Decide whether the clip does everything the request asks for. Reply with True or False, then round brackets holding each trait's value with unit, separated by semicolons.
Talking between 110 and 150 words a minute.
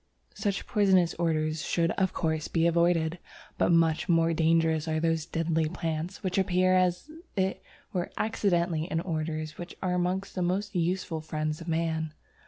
False (160 wpm)